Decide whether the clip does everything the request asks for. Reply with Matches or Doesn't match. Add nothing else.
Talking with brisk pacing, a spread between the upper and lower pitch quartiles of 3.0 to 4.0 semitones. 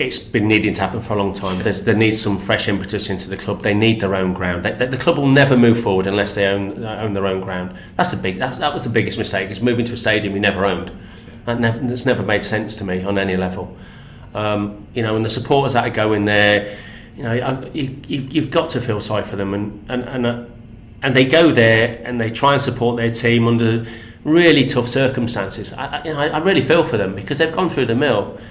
Matches